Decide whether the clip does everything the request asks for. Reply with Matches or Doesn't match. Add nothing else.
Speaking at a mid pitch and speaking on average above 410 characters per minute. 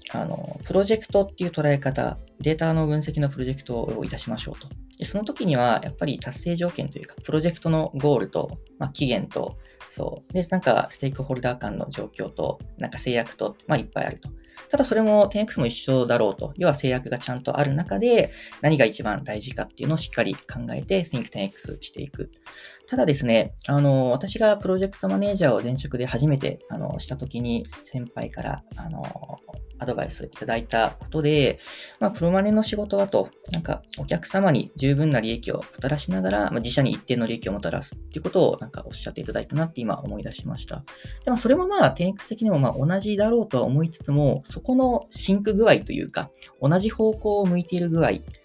Matches